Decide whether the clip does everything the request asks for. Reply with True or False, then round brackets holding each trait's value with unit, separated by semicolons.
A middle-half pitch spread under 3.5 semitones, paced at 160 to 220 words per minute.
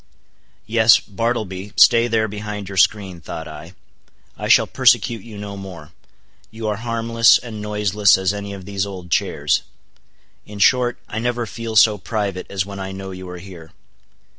True (2.8 semitones; 165 wpm)